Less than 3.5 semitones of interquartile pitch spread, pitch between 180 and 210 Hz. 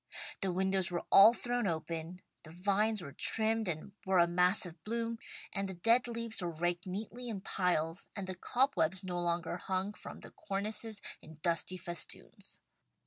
No: average, 4.0 semitones; high, 190 Hz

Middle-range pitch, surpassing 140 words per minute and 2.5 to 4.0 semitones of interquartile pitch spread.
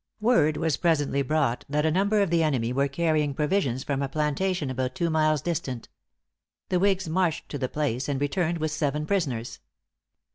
Yes: medium, 150 Hz; average, 180 wpm; average, 3.6 semitones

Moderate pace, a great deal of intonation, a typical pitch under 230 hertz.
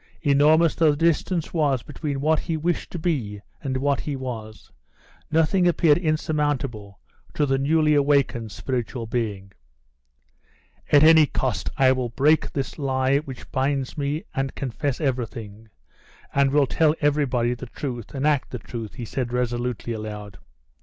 No: average, 150 wpm; average, 3.8 semitones; low, 135 Hz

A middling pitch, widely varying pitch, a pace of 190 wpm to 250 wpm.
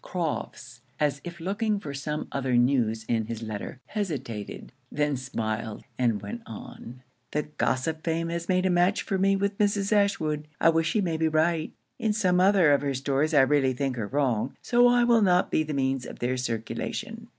Yes: medium, 150 Hz; wide, 6.2 semitones; average, 195 wpm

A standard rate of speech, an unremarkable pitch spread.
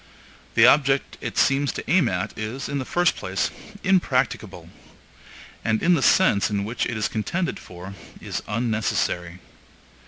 No: average, 150 wpm; wide, 6.1 semitones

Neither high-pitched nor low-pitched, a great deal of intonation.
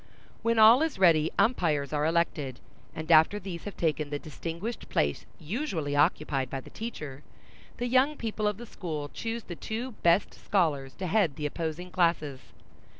Yes: medium, 170 Hz; wide, 6.4 semitones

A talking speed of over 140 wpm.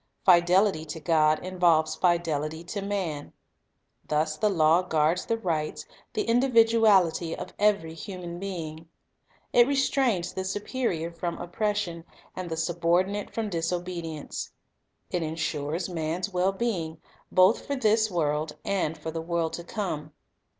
No: slow, 135 wpm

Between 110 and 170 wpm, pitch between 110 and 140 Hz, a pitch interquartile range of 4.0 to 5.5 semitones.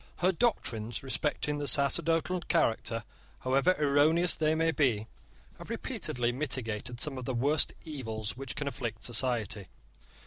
Yes: slow, 135 wpm; low, 135 Hz; average, 4.5 semitones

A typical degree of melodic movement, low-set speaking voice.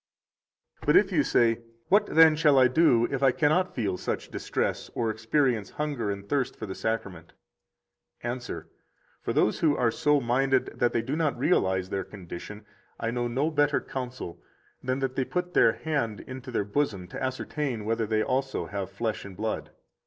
Yes: average, 4.7 semitones; low, 125 Hz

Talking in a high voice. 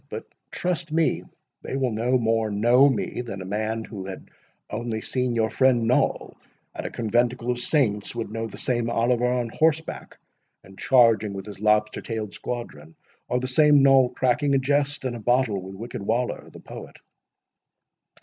No: low, 120 Hz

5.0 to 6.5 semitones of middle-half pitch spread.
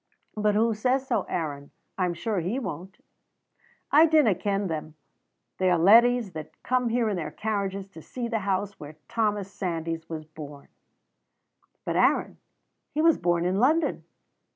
Yes: wide, 5.4 semitones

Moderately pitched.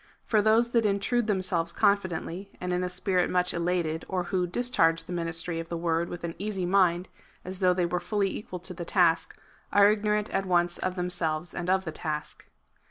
Yes: medium, 180 Hz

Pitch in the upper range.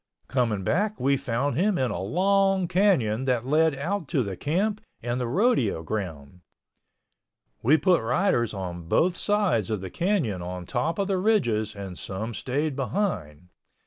No: low, 130 Hz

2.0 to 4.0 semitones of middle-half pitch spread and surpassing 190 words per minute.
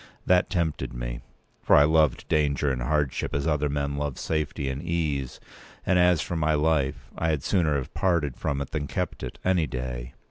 Yes: average, 2.7 semitones; average, 200 wpm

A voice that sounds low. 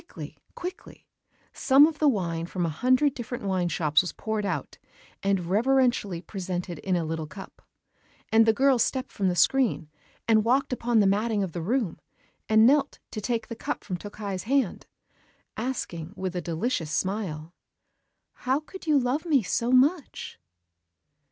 No: high, 215 Hz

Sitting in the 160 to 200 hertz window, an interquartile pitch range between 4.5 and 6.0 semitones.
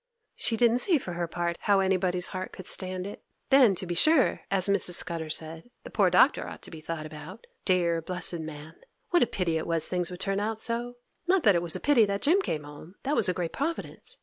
Yes: medium, 185 Hz; average, 4.8 semitones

